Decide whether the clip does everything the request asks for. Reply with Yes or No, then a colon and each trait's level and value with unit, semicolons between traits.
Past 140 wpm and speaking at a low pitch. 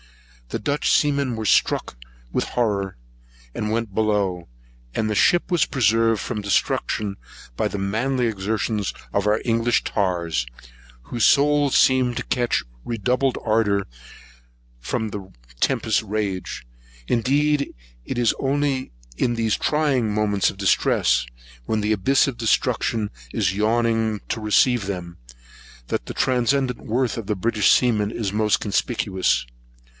No: slow, 135 wpm; low, 110 Hz